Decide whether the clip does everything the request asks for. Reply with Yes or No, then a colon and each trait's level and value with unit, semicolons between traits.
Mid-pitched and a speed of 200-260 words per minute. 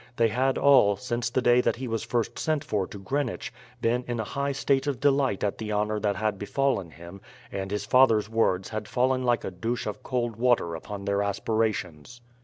No: low, 115 Hz; fast, 205 wpm